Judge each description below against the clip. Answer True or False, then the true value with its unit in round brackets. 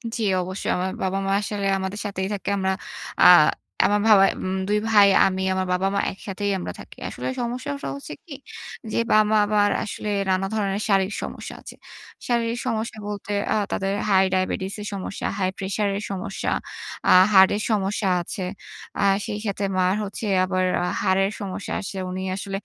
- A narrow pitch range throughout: True (1.7 semitones)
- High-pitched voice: True (195 Hz)